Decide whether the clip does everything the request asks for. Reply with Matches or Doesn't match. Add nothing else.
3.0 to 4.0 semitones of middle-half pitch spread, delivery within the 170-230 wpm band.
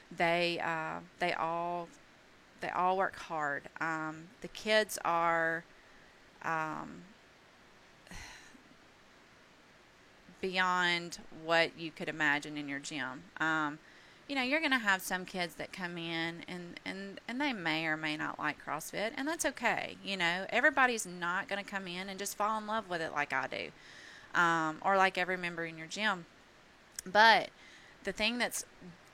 Doesn't match